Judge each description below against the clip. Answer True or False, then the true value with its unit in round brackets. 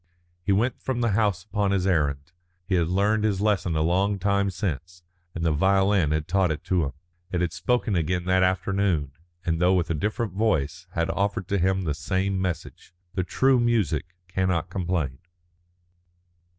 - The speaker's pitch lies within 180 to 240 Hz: False (95 Hz)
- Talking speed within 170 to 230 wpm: True (175 wpm)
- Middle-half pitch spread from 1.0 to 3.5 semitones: True (3.0 semitones)